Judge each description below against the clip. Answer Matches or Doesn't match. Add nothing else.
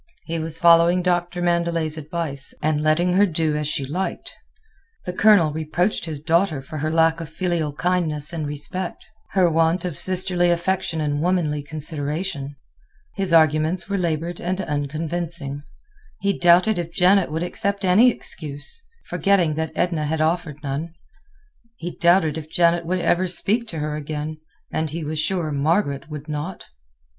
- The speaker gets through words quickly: Doesn't match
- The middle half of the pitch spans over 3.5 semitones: Doesn't match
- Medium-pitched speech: Matches